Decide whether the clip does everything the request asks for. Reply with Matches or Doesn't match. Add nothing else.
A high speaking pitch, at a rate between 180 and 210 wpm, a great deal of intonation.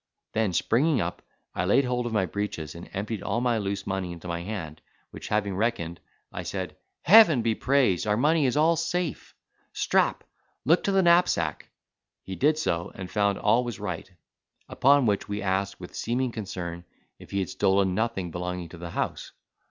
Doesn't match